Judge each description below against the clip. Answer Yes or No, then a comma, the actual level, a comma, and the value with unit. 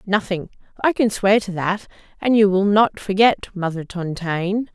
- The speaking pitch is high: Yes, high, 200 Hz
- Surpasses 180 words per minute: No, average, 165 wpm